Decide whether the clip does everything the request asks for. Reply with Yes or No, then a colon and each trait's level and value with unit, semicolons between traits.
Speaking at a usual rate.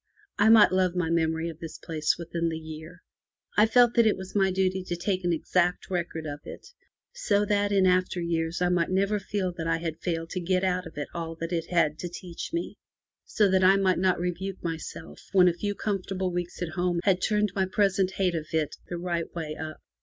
No: fast, 225 wpm